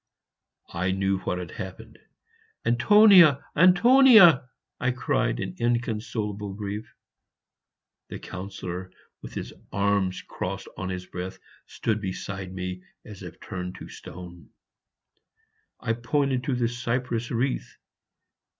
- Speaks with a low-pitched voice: Yes, low, 105 Hz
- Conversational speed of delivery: No, slow, 115 wpm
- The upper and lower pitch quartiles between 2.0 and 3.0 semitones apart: No, average, 5.2 semitones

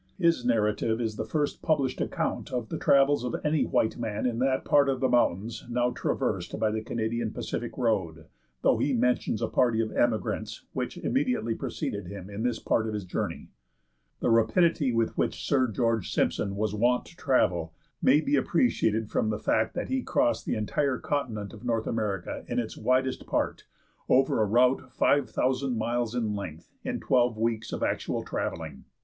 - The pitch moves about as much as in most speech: Yes, average, 3.2 semitones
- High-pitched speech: No, low, 120 Hz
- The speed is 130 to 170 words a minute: No, average, 180 wpm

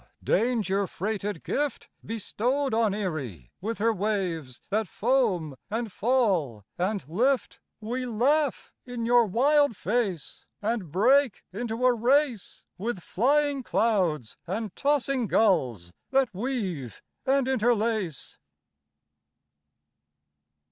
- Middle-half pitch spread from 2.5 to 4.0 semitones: No, average, 5.2 semitones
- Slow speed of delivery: Yes, slow, 105 wpm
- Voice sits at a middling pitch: No, high, 220 Hz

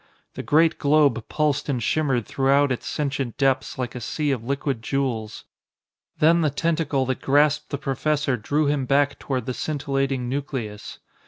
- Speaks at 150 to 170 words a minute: Yes, average, 160 wpm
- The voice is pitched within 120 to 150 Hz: Yes, medium, 140 Hz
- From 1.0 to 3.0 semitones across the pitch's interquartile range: Yes, narrow, 2.4 semitones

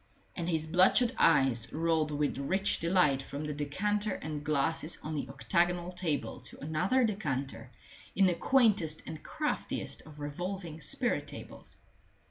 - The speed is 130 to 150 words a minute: Yes, average, 140 wpm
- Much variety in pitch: No, average, 4.1 semitones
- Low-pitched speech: No, medium, 160 Hz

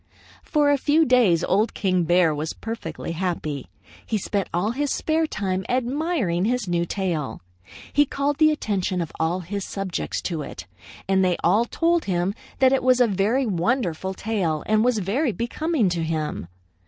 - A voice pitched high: Yes, high, 200 Hz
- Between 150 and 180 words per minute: Yes, average, 170 wpm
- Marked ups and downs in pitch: Yes, wide, 6.5 semitones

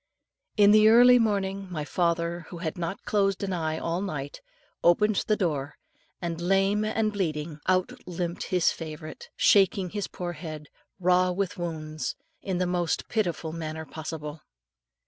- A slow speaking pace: No, average, 160 wpm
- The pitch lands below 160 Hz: No, medium, 175 Hz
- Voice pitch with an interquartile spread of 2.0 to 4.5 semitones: Yes, average, 3.5 semitones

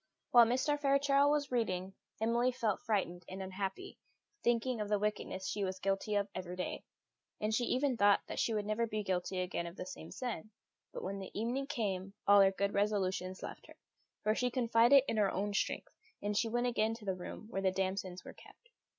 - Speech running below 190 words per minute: No, fast, 205 wpm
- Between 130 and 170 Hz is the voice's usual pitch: No, high, 210 Hz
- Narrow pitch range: No, average, 3.9 semitones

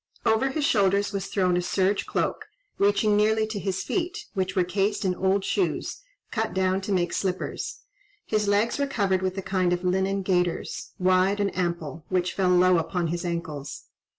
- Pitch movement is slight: Yes, narrow, 2.1 semitones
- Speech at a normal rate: Yes, average, 180 wpm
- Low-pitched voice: No, high, 190 Hz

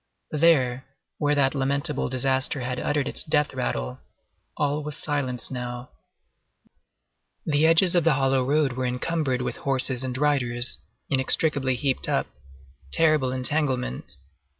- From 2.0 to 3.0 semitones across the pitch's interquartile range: Yes, average, 2.7 semitones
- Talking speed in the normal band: No, slow, 125 wpm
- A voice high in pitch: No, low, 135 Hz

